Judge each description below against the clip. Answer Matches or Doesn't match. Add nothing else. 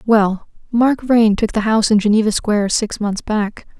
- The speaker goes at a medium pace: Matches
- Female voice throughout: Matches